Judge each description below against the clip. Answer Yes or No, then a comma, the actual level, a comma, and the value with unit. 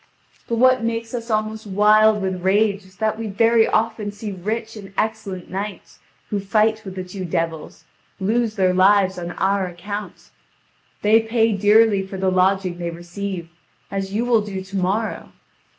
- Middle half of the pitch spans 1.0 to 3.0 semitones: Yes, narrow, 2.6 semitones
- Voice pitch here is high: Yes, high, 205 Hz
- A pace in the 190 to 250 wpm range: No, average, 165 wpm